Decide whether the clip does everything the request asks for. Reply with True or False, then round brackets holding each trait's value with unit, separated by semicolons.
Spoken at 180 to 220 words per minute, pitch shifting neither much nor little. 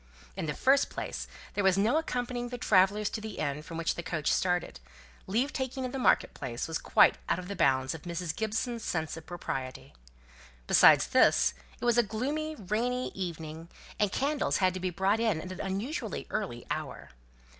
False (190 wpm; 6.5 semitones)